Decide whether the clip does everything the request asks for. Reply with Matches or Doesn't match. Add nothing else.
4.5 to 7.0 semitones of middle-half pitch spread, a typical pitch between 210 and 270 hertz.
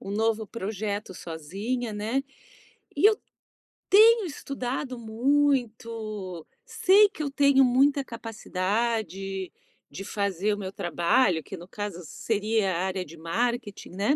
Matches